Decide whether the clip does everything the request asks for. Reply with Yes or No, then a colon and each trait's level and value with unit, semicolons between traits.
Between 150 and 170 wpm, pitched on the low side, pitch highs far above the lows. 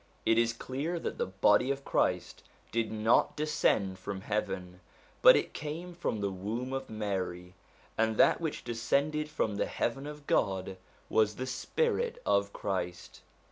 Yes: average, 155 wpm; low, 115 Hz; wide, 6.0 semitones